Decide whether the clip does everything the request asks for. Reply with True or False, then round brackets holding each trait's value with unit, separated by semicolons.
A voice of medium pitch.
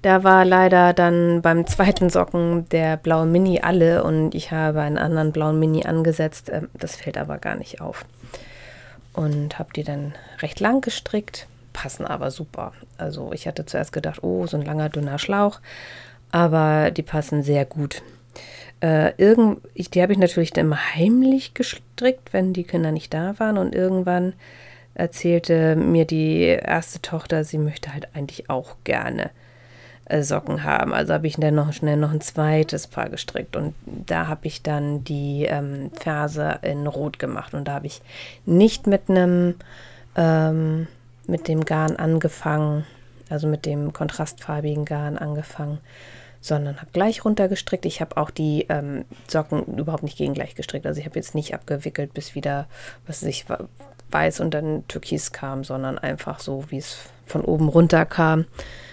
True (155 Hz)